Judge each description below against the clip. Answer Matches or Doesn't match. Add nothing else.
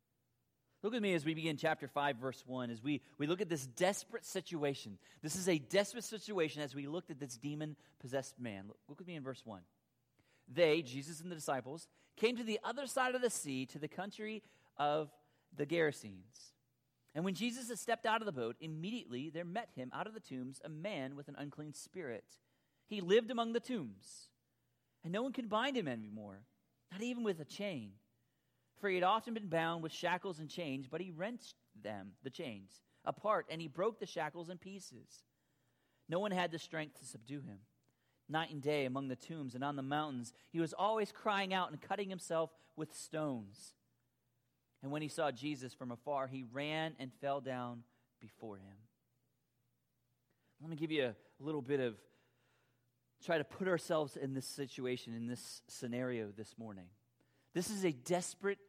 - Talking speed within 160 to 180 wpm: Doesn't match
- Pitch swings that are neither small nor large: Doesn't match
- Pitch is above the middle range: Doesn't match